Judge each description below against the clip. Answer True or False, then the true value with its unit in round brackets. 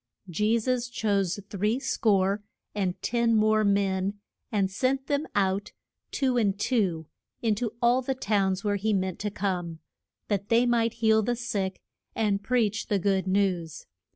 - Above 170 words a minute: False (155 wpm)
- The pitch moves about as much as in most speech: True (3.2 semitones)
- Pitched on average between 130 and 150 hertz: False (210 Hz)